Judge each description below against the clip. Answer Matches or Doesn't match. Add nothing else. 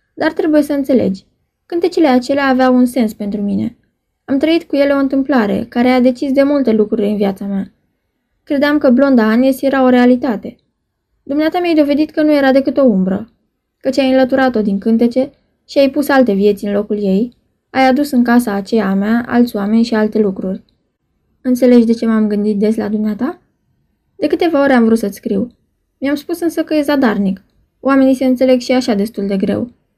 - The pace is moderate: Doesn't match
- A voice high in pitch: Matches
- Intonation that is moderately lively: Matches